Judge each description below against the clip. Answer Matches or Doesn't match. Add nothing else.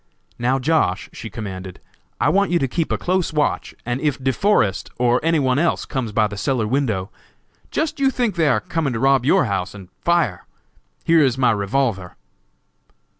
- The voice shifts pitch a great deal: Matches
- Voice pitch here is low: Matches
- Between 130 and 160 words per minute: Doesn't match